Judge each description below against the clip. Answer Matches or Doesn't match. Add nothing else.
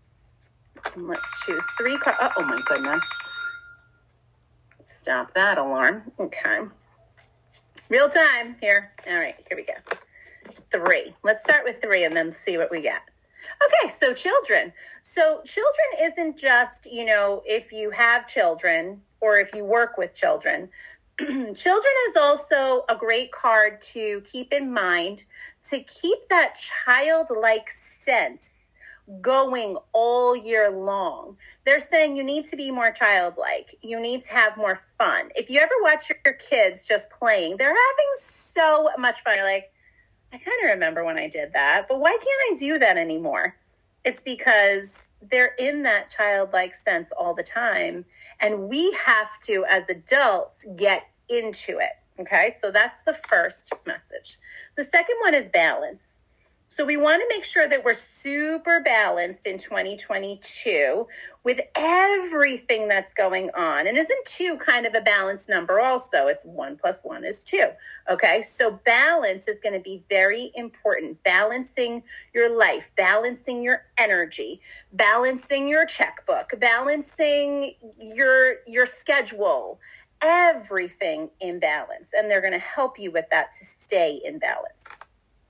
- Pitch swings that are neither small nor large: Doesn't match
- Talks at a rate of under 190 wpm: Matches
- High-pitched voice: Matches